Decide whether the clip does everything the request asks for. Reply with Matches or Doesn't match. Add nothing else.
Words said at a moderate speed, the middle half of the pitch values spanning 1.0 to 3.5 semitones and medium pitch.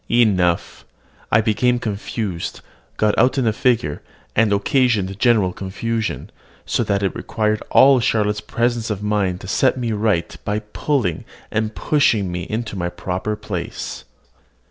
Doesn't match